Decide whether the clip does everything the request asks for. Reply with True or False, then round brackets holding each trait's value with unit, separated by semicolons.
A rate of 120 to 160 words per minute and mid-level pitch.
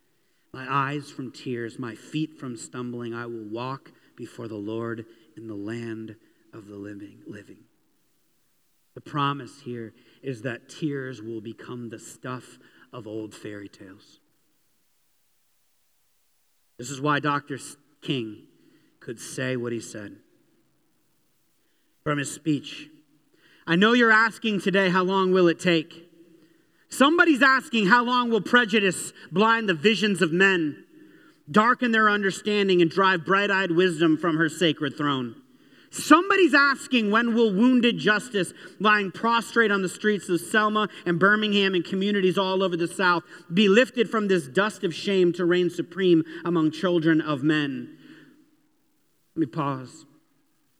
True (140 wpm; 175 Hz)